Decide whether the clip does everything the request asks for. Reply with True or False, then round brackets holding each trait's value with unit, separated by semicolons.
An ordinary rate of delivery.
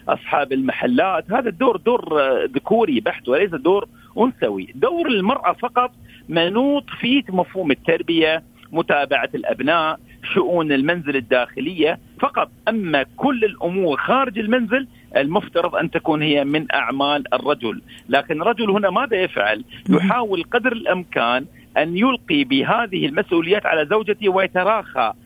True (120 wpm)